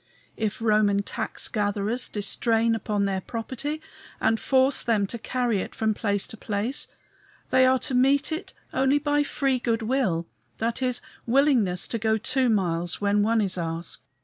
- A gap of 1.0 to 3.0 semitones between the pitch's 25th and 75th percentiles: No, average, 4.2 semitones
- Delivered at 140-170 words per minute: Yes, average, 165 wpm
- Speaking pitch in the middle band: No, high, 225 Hz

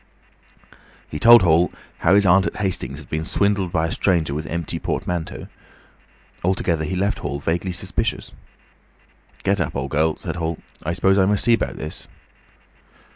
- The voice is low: Yes, very low, 85 Hz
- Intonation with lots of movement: No, average, 3.5 semitones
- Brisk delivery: No, average, 165 wpm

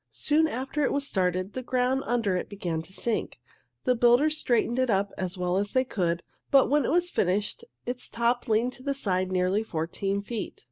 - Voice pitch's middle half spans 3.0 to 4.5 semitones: No, wide, 5.5 semitones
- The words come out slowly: No, average, 200 wpm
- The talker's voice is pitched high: Yes, high, 230 Hz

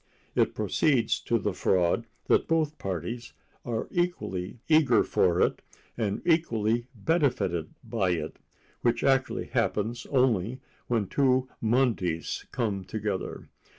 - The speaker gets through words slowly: Yes, slow, 115 wpm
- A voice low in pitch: Yes, low, 115 Hz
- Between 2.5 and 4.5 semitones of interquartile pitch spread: No, average, 5.0 semitones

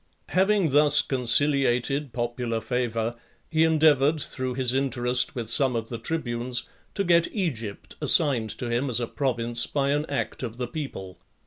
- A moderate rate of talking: Yes, average, 160 wpm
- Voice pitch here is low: Yes, low, 130 Hz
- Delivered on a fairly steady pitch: No, average, 3.7 semitones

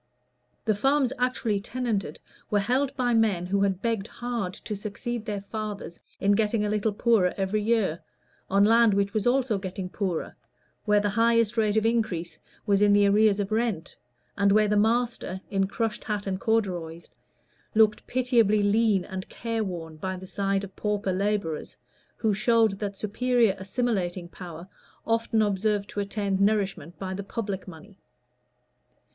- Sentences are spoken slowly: No, average, 160 wpm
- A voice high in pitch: Yes, high, 205 Hz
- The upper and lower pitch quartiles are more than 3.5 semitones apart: No, narrow, 2.6 semitones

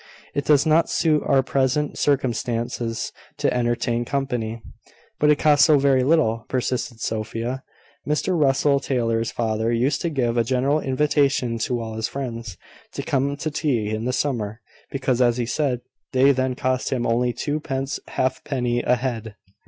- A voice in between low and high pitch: No, low, 130 Hz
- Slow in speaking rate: No, average, 160 wpm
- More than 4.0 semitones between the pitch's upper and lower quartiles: No, average, 3.1 semitones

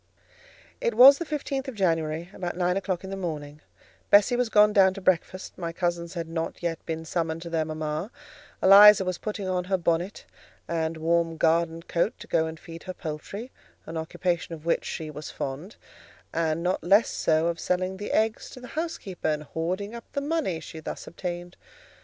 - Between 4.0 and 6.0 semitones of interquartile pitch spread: No, average, 3.3 semitones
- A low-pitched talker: No, medium, 175 Hz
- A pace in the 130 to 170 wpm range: No, average, 190 wpm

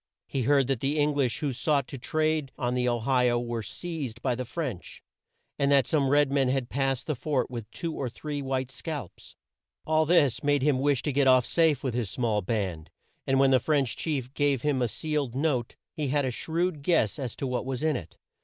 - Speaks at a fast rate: Yes, fast, 225 wpm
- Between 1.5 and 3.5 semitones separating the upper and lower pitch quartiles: Yes, average, 3.0 semitones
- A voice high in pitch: No, low, 135 Hz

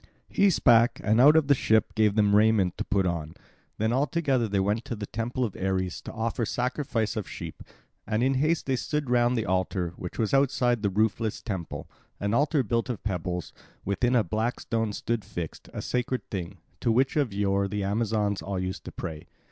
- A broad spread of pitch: No, average, 3.9 semitones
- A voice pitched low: Yes, low, 110 Hz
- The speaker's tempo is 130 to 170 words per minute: No, fast, 205 wpm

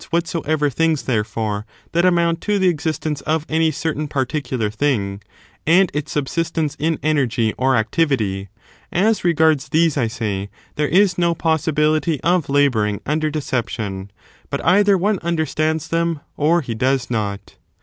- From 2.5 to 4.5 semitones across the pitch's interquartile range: No, average, 5.1 semitones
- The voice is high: No, medium, 150 Hz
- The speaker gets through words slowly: No, average, 145 wpm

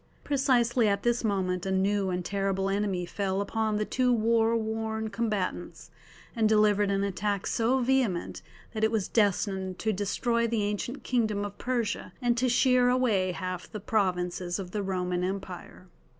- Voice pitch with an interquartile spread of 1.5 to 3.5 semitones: Yes, average, 3.2 semitones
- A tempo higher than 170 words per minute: No, average, 165 wpm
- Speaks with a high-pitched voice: Yes, high, 210 Hz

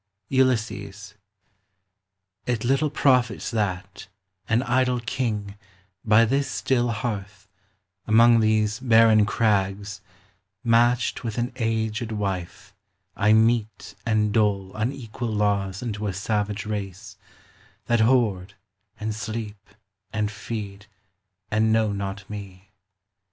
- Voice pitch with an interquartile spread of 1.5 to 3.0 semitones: Yes, narrow, 2.5 semitones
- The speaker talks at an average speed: No, slow, 105 wpm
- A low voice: Yes, low, 110 Hz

